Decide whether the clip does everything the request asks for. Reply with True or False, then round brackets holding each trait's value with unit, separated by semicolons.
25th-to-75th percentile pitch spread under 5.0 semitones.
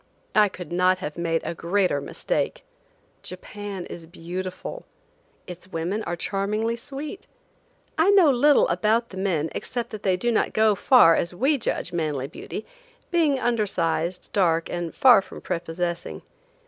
False (5.4 semitones)